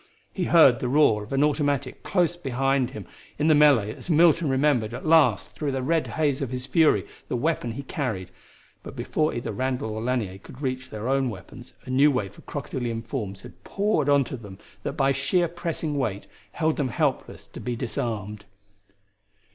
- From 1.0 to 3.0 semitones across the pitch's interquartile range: No, average, 4.5 semitones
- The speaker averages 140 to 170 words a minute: No, average, 185 wpm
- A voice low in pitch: Yes, low, 130 Hz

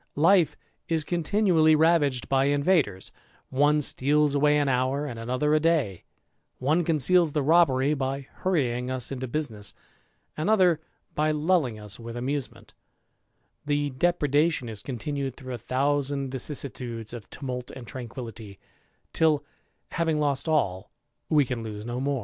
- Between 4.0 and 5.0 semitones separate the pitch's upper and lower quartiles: No, average, 3.6 semitones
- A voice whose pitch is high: No, medium, 140 Hz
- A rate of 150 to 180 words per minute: No, average, 140 wpm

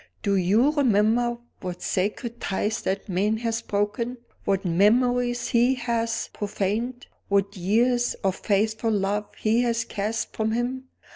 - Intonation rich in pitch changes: No, average, 3.1 semitones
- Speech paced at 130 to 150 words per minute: Yes, slow, 135 wpm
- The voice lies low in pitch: No, high, 220 Hz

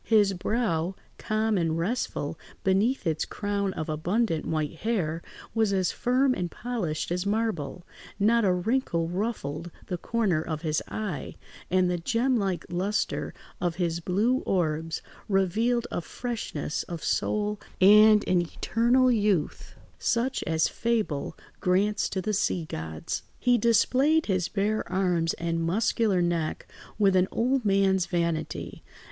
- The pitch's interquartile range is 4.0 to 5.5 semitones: Yes, average, 4.8 semitones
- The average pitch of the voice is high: Yes, high, 195 Hz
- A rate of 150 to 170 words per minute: No, average, 140 wpm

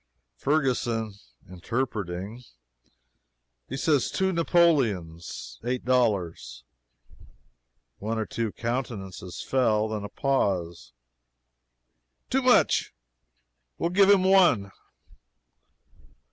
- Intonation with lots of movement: Yes, wide, 6.1 semitones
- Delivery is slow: Yes, slow, 85 wpm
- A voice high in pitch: No, low, 115 Hz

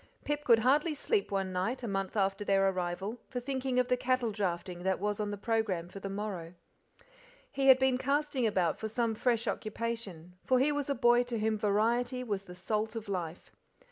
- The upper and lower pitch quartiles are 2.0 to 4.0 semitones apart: No, average, 4.5 semitones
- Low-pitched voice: No, high, 220 Hz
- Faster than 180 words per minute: Yes, fast, 205 wpm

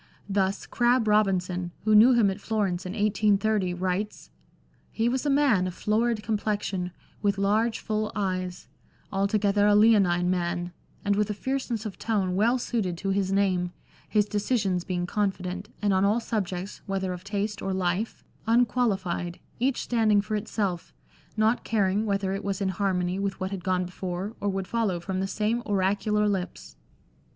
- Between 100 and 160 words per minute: No, average, 175 wpm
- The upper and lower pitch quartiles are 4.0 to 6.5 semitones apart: No, narrow, 2.5 semitones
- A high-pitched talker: Yes, high, 200 Hz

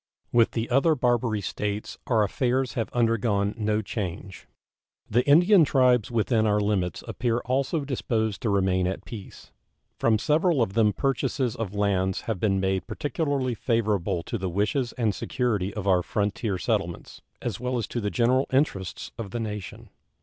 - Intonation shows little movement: No, average, 3.8 semitones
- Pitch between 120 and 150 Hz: No, low, 110 Hz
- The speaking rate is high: No, average, 165 wpm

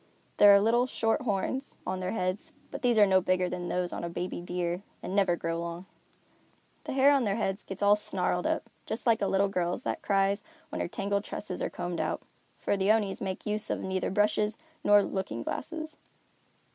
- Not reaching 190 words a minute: No, fast, 205 wpm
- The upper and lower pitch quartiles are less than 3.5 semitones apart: Yes, average, 2.8 semitones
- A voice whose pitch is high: Yes, high, 195 Hz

